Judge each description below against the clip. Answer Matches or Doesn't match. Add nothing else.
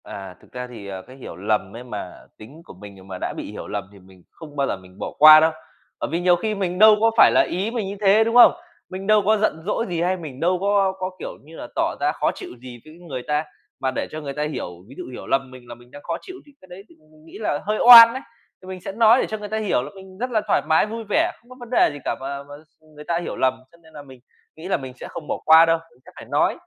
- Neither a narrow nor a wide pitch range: Doesn't match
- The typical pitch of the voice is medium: Matches